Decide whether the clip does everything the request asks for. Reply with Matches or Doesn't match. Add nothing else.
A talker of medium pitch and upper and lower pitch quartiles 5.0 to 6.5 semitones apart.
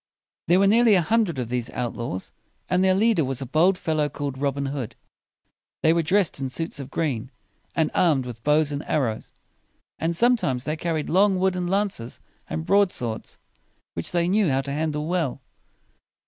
Matches